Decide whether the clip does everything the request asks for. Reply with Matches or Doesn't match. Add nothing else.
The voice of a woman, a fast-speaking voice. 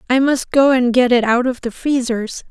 Matches